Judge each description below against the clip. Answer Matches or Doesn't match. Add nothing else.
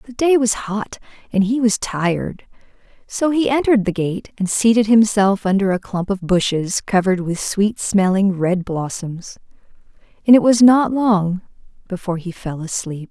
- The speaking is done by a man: Doesn't match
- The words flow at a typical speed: Matches